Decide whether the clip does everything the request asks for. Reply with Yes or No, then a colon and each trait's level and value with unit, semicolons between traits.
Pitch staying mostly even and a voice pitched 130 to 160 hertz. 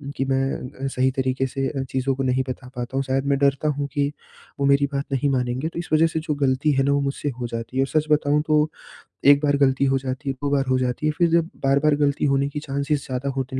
Yes: narrow, 1.6 semitones; medium, 140 Hz